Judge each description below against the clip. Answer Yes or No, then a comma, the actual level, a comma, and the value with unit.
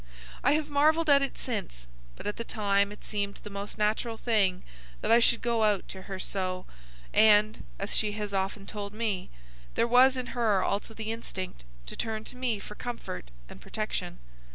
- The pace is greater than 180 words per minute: Yes, average, 190 wpm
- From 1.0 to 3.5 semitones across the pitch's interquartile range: Yes, average, 2.8 semitones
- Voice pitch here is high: Yes, high, 215 Hz